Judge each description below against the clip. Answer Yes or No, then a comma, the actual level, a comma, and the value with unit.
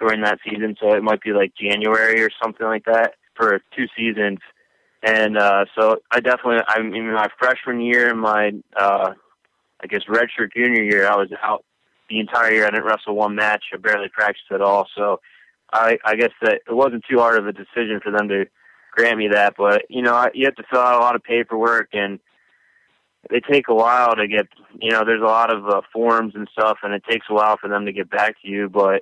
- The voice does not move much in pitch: Yes, narrow, 2.0 semitones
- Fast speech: Yes, fast, 230 wpm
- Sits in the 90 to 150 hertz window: Yes, low, 110 Hz